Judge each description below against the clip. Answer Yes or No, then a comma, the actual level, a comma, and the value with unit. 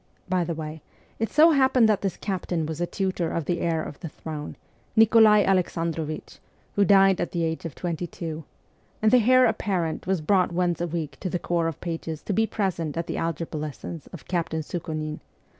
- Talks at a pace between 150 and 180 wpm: No, average, 200 wpm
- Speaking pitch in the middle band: Yes, medium, 175 Hz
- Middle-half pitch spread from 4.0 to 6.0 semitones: No, average, 3.2 semitones